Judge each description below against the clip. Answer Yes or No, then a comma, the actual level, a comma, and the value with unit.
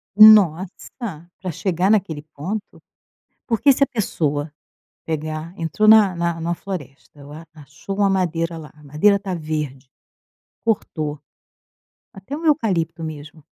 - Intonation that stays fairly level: No, average, 4.6 semitones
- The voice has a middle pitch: Yes, medium, 170 Hz